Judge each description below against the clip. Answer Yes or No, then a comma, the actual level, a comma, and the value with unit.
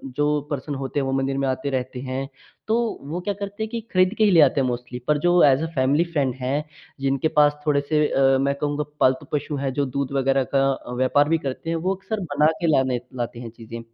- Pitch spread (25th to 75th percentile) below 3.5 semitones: Yes, average, 3.0 semitones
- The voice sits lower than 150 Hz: Yes, medium, 140 Hz